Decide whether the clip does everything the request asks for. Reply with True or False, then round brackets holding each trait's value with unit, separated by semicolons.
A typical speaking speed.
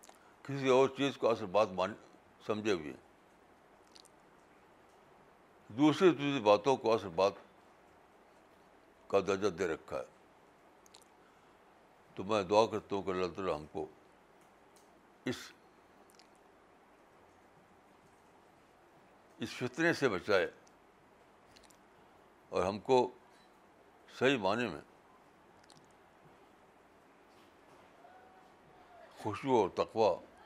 False (85 wpm)